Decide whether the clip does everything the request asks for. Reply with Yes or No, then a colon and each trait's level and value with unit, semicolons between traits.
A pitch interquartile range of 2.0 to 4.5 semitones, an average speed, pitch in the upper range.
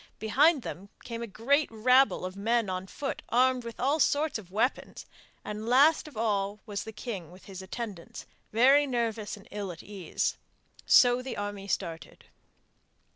Yes: average, 4.2 semitones; average, 165 wpm; high, 220 Hz